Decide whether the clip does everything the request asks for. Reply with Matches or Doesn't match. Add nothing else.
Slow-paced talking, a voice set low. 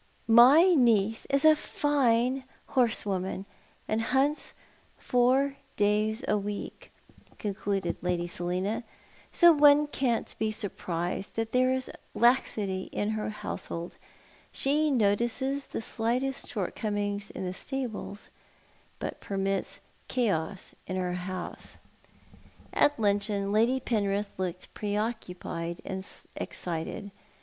Doesn't match